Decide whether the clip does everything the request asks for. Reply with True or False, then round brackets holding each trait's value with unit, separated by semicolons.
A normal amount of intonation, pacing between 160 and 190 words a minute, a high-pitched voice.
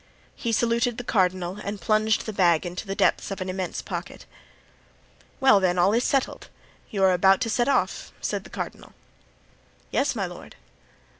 True (4.0 semitones; 165 wpm; 200 Hz)